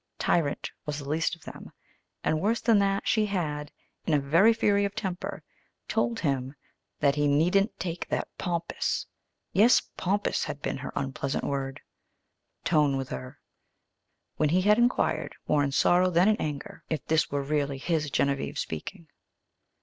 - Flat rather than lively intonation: No, wide, 5.6 semitones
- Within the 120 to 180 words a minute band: Yes, average, 160 wpm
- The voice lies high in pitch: No, medium, 160 Hz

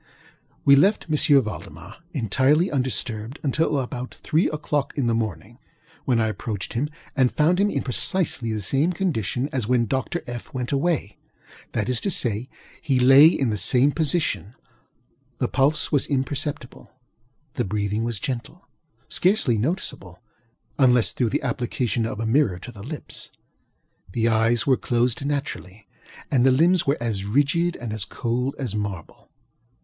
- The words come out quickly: No, average, 155 wpm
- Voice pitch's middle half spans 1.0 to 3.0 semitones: No, average, 4.5 semitones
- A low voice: Yes, low, 125 Hz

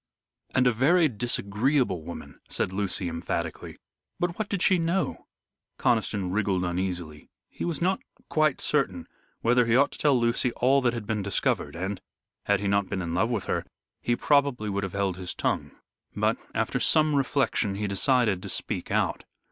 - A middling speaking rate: Yes, average, 175 wpm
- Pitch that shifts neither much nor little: No, wide, 6.2 semitones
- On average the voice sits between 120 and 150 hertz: No, low, 110 Hz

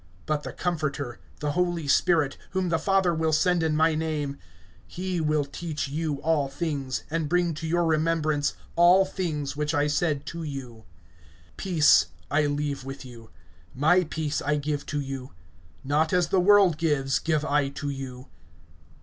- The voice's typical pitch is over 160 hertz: No, medium, 155 Hz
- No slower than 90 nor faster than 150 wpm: No, average, 165 wpm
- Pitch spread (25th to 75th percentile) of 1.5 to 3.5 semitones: Yes, average, 2.8 semitones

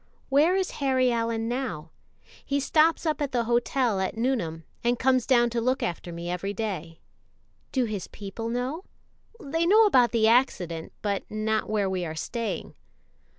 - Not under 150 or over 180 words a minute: Yes, average, 165 wpm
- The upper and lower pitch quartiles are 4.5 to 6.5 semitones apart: Yes, average, 4.9 semitones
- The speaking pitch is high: Yes, high, 235 Hz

